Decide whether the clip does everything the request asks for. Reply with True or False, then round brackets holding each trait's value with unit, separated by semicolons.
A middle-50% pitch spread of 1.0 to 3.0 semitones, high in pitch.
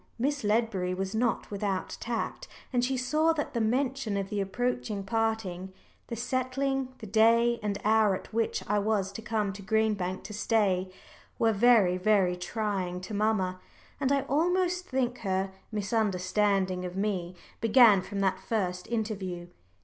False (3.8 semitones; 215 Hz)